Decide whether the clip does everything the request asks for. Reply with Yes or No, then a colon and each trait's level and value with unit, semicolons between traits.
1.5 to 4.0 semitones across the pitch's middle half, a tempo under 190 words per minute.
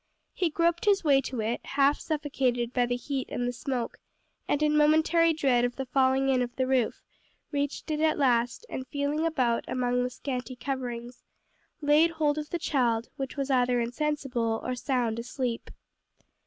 Yes: average, 3.3 semitones; average, 170 wpm